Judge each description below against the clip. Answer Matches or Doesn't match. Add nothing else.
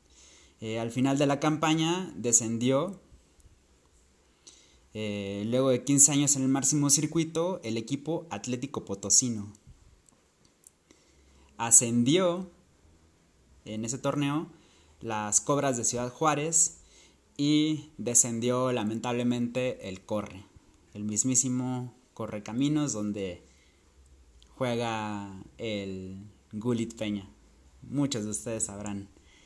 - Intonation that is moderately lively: Doesn't match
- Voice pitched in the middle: Doesn't match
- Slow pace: Matches